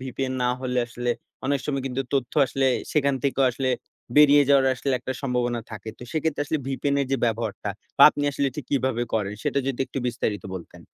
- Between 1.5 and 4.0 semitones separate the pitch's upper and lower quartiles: Yes, narrow, 2.5 semitones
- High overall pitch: No, low, 130 Hz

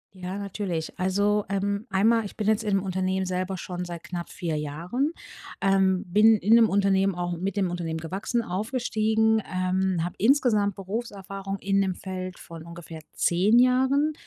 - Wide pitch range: No, average, 2.9 semitones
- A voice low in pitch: No, high, 195 Hz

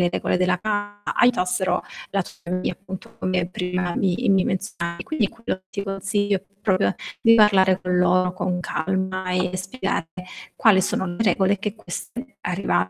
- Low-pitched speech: No, high, 190 Hz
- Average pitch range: No, narrow, 2.0 semitones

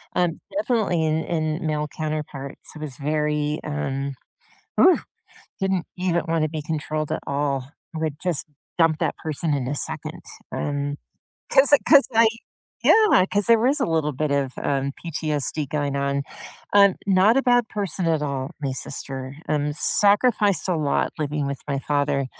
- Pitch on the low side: No, medium, 155 Hz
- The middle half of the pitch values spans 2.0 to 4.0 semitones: No, average, 4.4 semitones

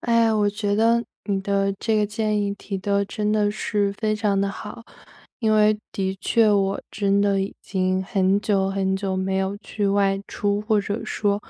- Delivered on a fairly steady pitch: Yes, narrow, 1.4 semitones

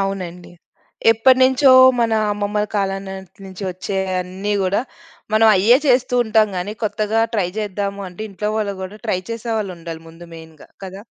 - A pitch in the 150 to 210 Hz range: Yes, high, 200 Hz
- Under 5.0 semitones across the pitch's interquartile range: Yes, average, 2.8 semitones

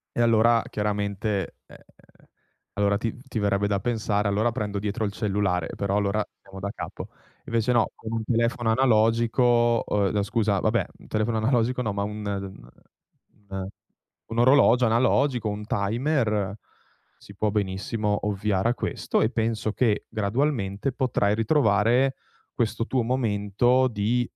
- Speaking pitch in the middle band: No, low, 110 Hz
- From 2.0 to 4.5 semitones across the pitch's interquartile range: Yes, narrow, 2.6 semitones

